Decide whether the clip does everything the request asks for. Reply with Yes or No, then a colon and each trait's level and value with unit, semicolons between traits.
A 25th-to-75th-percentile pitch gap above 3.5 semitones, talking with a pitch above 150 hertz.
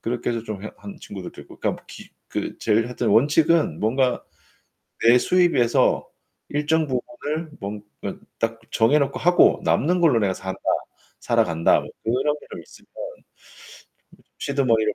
No: average, 5.3 semitones; low, 125 Hz